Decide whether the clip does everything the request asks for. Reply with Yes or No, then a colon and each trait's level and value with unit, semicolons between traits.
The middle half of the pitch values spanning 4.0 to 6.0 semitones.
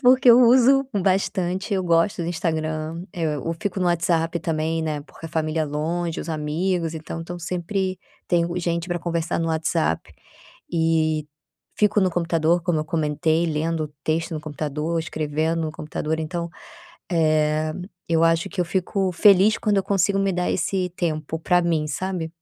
No: narrow, 2.4 semitones